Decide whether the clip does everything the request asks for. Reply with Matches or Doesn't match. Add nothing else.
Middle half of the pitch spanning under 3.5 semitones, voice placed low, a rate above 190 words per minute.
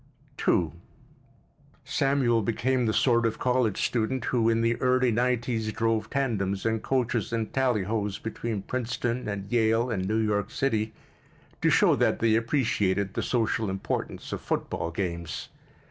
Doesn't match